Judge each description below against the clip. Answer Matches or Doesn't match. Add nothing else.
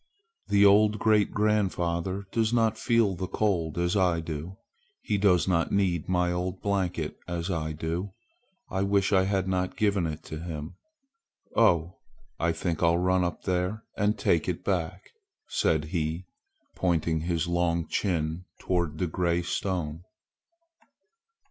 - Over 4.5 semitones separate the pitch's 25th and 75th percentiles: Doesn't match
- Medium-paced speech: Matches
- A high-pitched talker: Doesn't match